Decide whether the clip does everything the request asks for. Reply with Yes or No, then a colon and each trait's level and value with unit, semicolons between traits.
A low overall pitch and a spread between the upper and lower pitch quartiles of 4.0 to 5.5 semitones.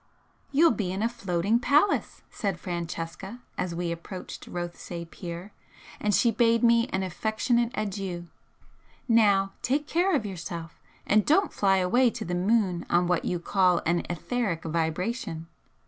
No: high, 195 Hz; average, 5.0 semitones